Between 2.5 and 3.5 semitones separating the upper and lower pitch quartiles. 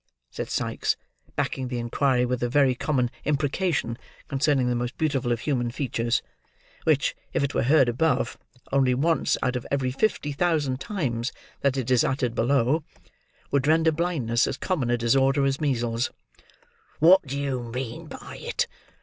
Yes: average, 3.2 semitones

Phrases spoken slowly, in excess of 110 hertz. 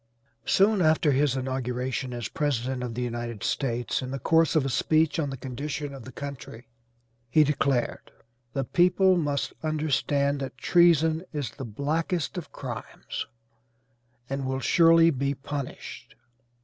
No: average, 145 wpm; medium, 140 Hz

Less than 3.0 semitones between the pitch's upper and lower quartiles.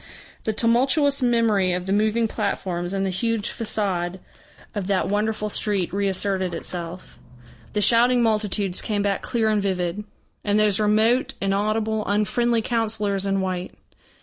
Yes: narrow, 2.5 semitones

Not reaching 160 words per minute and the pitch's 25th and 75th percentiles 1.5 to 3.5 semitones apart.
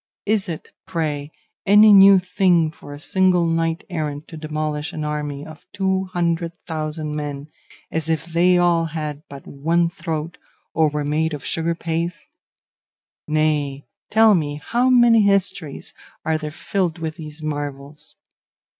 Yes: average, 145 wpm; average, 2.8 semitones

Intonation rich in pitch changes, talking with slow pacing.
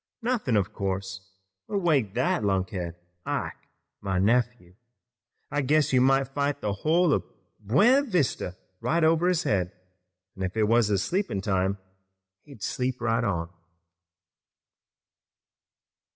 Yes: wide, 7.5 semitones; slow, 130 wpm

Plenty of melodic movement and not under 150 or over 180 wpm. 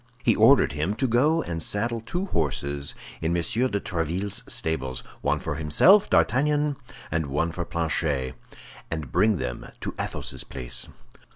No: wide, 7.8 semitones; slow, 135 wpm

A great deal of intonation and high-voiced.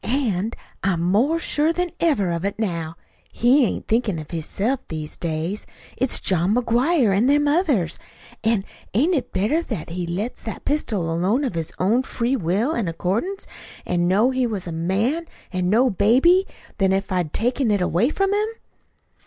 Yes: wide, 6.7 semitones; high, 220 Hz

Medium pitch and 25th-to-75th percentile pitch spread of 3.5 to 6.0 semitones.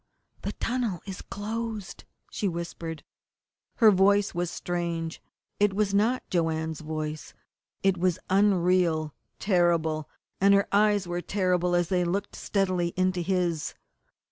No: medium, 180 Hz; average, 2.8 semitones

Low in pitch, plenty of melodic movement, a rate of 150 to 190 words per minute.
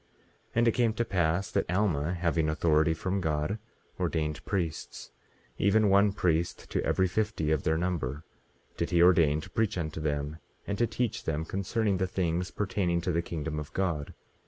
No: very low, 85 Hz; average, 3.9 semitones; average, 180 wpm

